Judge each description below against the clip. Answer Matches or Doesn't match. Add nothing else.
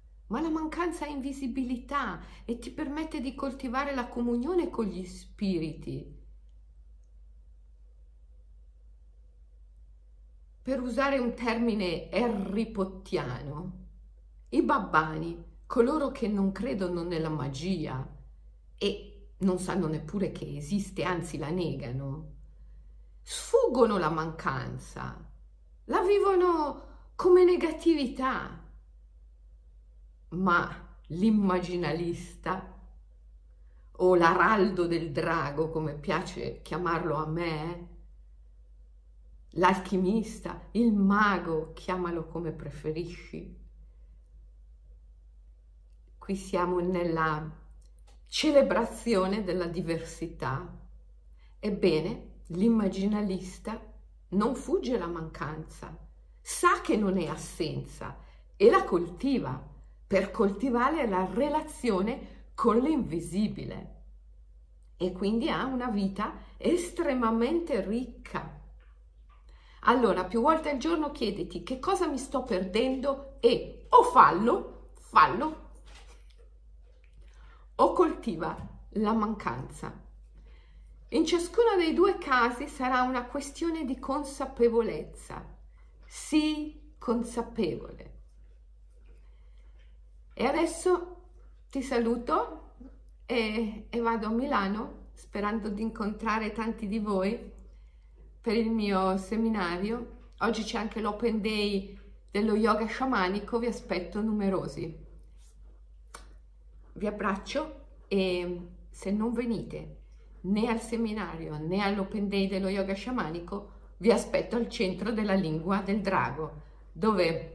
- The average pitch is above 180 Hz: Matches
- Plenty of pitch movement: Matches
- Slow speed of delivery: Matches